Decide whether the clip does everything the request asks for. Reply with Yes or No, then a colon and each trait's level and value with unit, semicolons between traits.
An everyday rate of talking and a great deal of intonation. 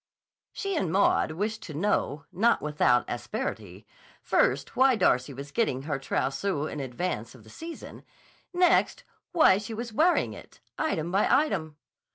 Yes: average, 150 wpm; wide, 8.8 semitones